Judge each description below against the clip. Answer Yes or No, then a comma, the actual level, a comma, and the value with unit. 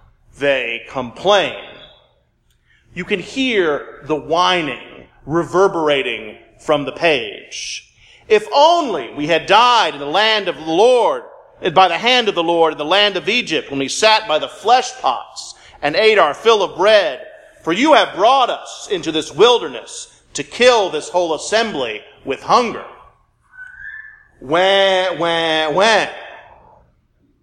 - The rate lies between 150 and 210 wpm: No, average, 140 wpm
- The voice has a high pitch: Yes, high, 205 Hz